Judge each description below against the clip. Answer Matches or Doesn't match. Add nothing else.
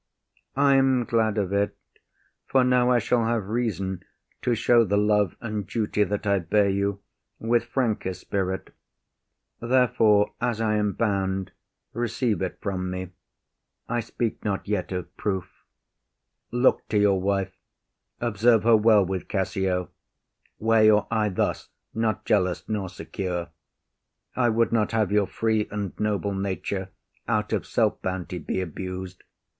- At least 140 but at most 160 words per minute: Matches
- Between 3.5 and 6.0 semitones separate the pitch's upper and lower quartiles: Doesn't match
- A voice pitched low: Matches